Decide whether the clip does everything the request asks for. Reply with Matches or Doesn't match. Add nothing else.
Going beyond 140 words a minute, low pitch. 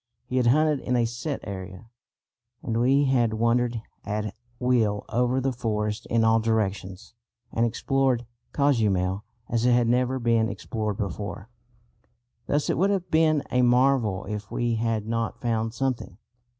Matches